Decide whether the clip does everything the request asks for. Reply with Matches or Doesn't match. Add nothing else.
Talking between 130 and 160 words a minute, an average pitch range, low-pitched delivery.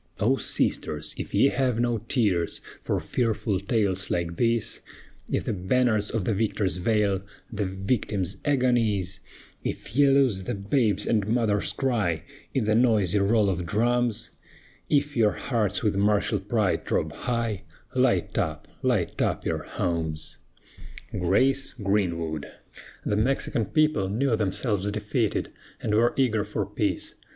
Matches